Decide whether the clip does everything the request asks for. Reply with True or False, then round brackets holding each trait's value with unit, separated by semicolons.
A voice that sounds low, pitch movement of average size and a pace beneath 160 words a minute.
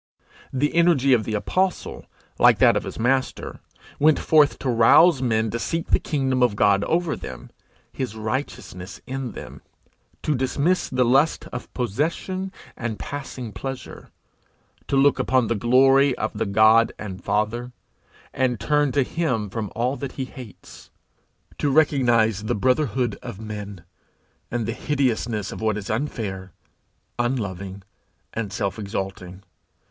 True (120 Hz; 4.3 semitones; 145 wpm)